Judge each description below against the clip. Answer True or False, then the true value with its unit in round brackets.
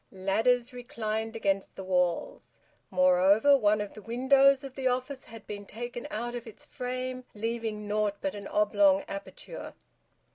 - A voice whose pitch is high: True (225 Hz)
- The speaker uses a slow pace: False (150 wpm)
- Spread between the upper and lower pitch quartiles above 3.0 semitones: True (3.7 semitones)